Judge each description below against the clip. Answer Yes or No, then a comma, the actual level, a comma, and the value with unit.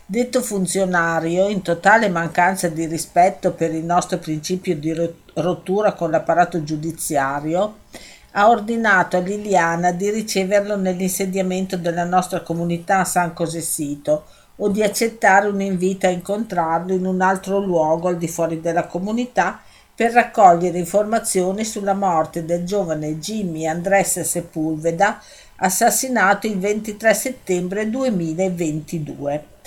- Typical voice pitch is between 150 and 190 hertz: Yes, medium, 185 Hz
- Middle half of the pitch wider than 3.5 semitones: No, average, 3.2 semitones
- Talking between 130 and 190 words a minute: No, average, 120 wpm